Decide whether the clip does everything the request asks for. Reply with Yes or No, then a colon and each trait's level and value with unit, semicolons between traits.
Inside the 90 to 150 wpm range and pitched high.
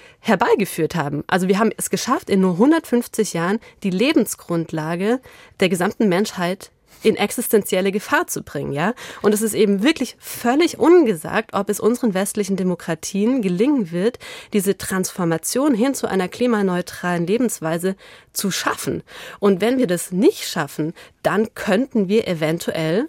Yes: average, 145 wpm; high, 205 Hz